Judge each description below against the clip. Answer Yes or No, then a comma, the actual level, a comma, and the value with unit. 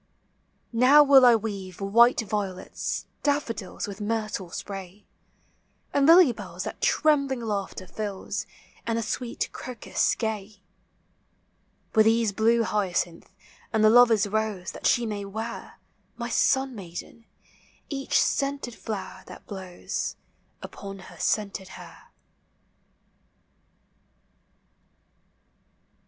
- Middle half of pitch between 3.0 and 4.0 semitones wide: Yes, average, 3.4 semitones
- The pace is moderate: No, slow, 105 wpm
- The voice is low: No, high, 220 Hz